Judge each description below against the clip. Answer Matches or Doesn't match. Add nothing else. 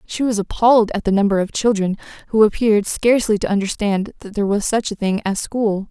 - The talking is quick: Matches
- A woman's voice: Matches